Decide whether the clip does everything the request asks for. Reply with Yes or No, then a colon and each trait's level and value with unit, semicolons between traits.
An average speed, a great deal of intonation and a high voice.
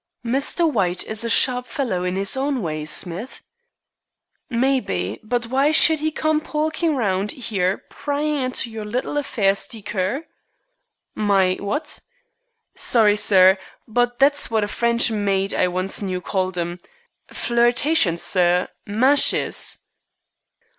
No: slow, 125 wpm; wide, 6.0 semitones; high, 220 Hz